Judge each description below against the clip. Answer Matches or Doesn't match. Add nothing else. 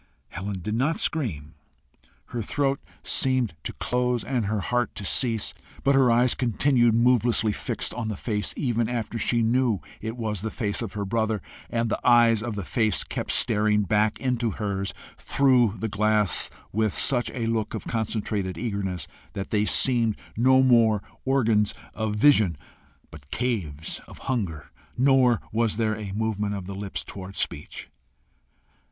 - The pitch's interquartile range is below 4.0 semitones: Matches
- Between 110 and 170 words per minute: Matches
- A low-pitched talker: Matches